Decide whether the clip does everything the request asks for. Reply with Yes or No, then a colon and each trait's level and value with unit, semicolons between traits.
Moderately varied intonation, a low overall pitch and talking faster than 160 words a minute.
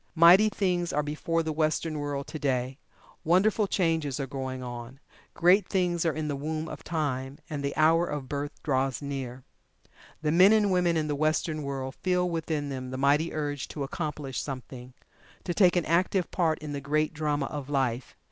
No: average, 3.5 semitones; medium, 150 Hz; average, 185 wpm